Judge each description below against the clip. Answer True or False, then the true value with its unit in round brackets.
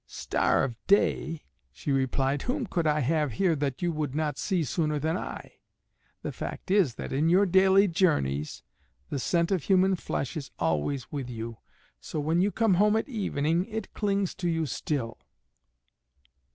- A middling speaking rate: True (170 wpm)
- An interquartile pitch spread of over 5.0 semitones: True (5.6 semitones)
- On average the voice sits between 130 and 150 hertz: False (160 Hz)